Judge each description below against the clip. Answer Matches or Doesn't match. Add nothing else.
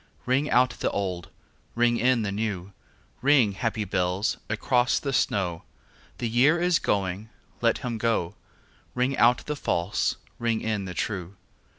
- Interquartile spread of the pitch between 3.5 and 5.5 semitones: Matches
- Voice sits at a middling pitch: Doesn't match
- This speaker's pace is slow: Doesn't match